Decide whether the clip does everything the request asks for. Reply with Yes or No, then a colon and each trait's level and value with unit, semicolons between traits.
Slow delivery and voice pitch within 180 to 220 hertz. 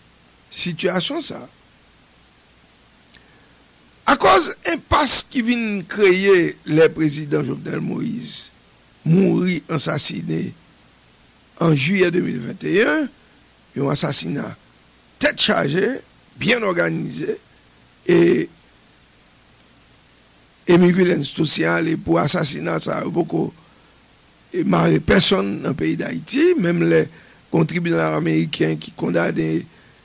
No: slow, 90 wpm; medium, 160 Hz